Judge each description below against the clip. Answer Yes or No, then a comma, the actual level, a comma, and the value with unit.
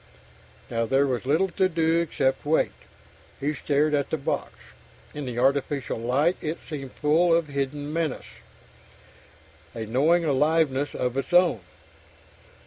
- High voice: No, medium, 145 Hz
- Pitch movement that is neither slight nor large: Yes, average, 3.3 semitones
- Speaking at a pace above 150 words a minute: No, slow, 135 wpm